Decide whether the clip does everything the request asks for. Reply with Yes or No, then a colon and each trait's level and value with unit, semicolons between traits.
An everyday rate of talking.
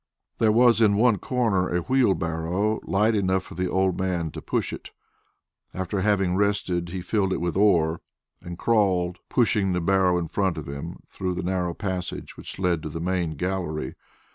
Yes: average, 180 wpm